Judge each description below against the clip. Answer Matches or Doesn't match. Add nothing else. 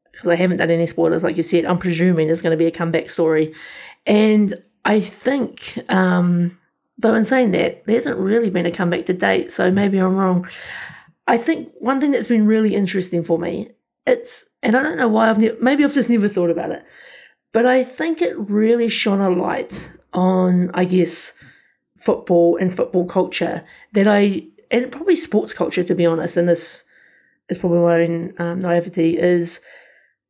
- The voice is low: Doesn't match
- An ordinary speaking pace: Matches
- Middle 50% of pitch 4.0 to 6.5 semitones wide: Matches